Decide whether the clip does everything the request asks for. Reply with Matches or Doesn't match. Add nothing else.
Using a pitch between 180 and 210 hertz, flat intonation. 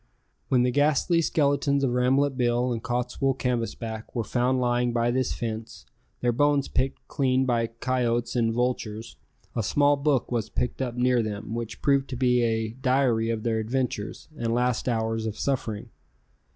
Doesn't match